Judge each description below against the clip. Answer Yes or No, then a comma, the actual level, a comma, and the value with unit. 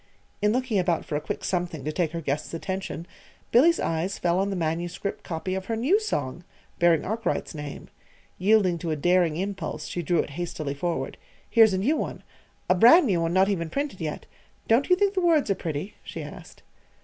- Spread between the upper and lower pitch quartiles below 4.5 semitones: No, average, 4.9 semitones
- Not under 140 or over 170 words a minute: No, average, 200 wpm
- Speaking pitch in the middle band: Yes, medium, 180 Hz